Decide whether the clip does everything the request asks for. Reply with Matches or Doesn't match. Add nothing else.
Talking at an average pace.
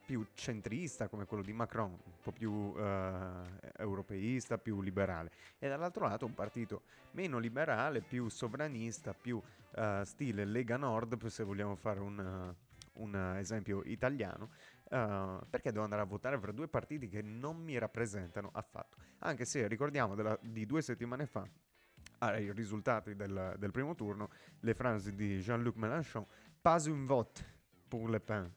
Matches